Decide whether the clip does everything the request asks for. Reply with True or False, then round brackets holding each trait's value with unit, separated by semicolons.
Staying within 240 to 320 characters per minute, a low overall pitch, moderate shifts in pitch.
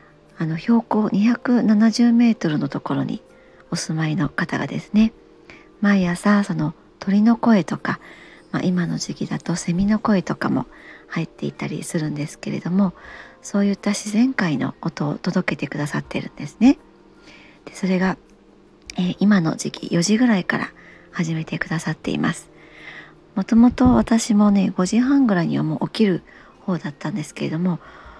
False (300 characters per minute; 185 Hz; 4.5 semitones)